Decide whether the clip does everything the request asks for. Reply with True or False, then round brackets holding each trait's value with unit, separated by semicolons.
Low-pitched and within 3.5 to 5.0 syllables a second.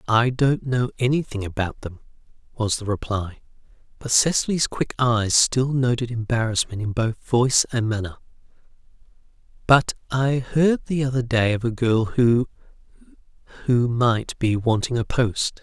True (120 Hz; 4.5 syllables/s)